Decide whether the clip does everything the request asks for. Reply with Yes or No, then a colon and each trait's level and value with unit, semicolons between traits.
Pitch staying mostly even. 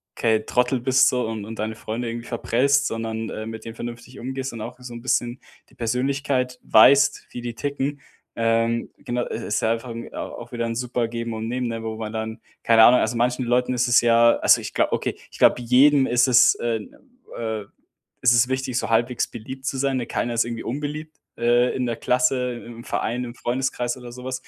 Yes: narrow, 1.7 semitones